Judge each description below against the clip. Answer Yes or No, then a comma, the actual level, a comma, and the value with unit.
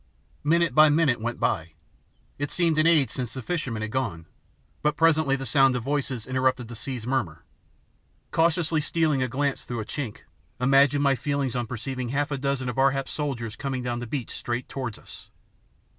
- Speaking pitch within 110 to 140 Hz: Yes, low, 135 Hz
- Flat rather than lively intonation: No, average, 3.2 semitones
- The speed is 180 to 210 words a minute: Yes, average, 190 wpm